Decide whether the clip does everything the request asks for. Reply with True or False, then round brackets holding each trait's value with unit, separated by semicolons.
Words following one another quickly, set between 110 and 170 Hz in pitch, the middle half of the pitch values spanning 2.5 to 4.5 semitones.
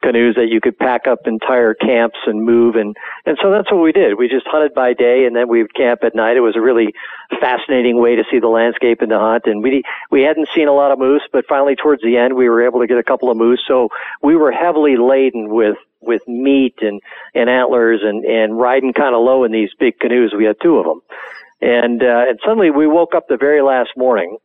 True (250 wpm; 125 Hz; 3.1 semitones)